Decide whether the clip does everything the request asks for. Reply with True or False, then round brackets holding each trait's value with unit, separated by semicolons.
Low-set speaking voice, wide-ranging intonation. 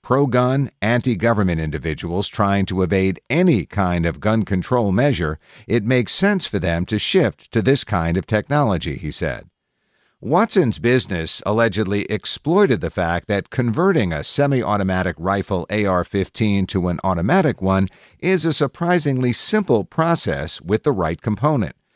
True (105 Hz; 6.3 semitones)